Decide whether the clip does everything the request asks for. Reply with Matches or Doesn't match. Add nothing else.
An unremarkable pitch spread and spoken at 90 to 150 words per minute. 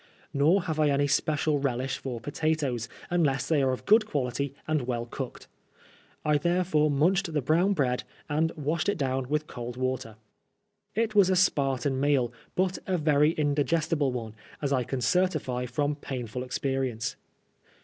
Doesn't match